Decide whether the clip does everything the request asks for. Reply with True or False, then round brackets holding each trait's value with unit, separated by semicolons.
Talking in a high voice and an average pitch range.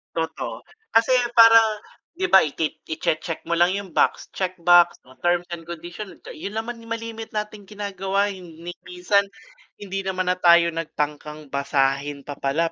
False (175 Hz; 4.0 semitones)